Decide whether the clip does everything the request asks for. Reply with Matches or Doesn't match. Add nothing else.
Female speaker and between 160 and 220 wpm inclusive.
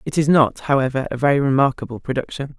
Matches